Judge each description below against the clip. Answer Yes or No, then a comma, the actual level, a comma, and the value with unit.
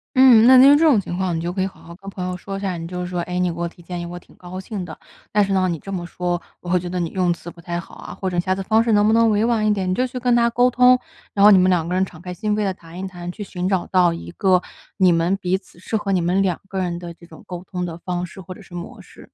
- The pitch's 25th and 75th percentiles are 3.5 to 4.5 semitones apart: No, narrow, 2.5 semitones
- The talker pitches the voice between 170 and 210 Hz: Yes, medium, 185 Hz